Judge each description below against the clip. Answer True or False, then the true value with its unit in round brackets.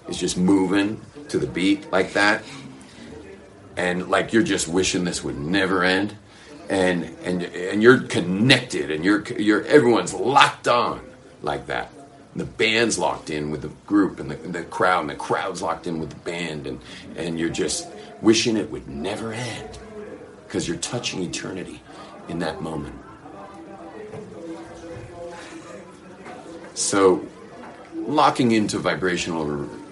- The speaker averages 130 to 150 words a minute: True (140 wpm)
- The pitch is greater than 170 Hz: False (95 Hz)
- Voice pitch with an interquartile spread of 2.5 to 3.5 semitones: False (4.3 semitones)